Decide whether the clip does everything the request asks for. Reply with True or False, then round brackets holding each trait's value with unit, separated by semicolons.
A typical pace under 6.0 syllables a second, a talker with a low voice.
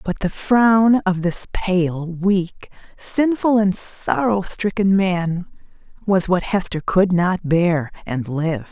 False (3.4 syllables/s; 185 Hz)